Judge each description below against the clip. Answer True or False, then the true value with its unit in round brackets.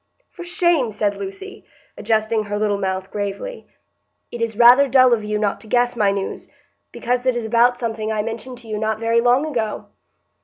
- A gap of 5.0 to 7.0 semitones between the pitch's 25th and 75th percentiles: False (2.8 semitones)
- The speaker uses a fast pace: False (195 wpm)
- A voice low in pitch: False (230 Hz)